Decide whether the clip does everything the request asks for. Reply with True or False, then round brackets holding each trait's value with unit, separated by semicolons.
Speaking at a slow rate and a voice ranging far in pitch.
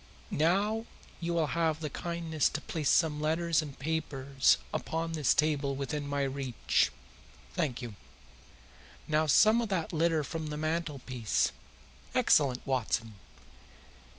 False (125 wpm; 3.1 semitones)